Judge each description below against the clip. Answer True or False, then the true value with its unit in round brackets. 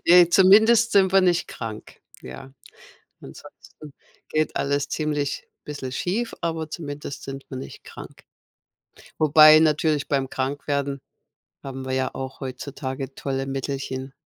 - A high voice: False (145 Hz)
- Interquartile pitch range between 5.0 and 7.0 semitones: False (3.1 semitones)